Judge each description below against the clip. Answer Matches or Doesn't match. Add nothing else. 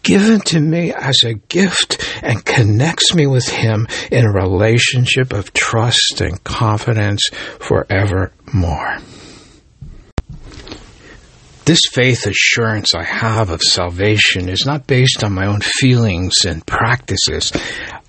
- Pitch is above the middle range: Doesn't match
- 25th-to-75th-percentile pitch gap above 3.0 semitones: Matches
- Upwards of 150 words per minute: Doesn't match